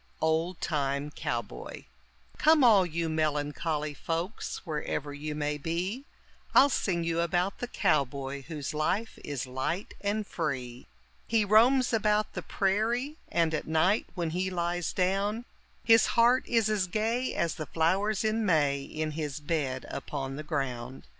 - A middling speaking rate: Yes, average, 145 wpm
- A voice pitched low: No, medium, 170 Hz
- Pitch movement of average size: No, wide, 6.1 semitones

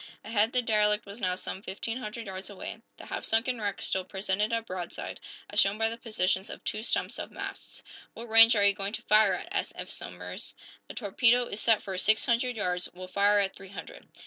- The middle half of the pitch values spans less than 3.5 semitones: Yes, average, 2.8 semitones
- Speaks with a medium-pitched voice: No, high, 210 Hz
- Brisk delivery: Yes, fast, 220 wpm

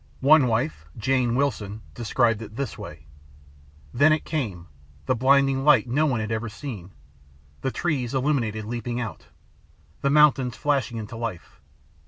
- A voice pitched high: No, low, 120 Hz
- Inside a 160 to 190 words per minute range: No, average, 145 wpm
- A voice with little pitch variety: No, average, 4.1 semitones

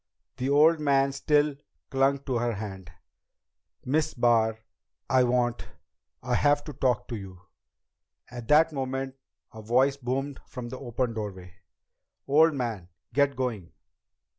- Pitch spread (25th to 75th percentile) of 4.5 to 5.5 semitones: No, average, 3.3 semitones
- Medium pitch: No, low, 130 Hz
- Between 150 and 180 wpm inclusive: No, average, 140 wpm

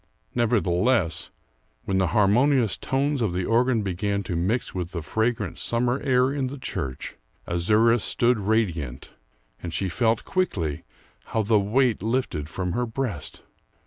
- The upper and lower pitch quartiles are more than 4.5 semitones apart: Yes, wide, 5.4 semitones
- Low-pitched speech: Yes, low, 110 Hz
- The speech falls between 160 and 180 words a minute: No, average, 145 wpm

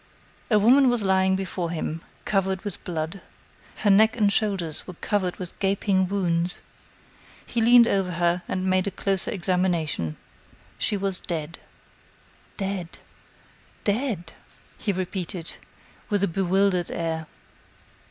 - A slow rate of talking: Yes, slow, 125 wpm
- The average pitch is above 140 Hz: Yes, high, 190 Hz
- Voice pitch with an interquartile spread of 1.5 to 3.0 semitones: Yes, narrow, 2.5 semitones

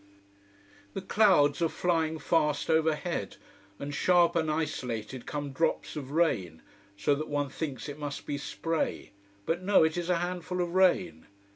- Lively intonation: No, average, 3.1 semitones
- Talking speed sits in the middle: Yes, average, 155 wpm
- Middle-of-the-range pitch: Yes, medium, 160 Hz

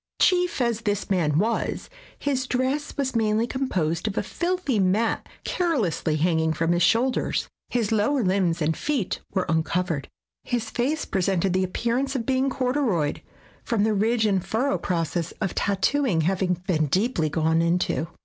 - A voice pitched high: Yes, high, 205 Hz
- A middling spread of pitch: No, wide, 6.7 semitones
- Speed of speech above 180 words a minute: No, average, 160 wpm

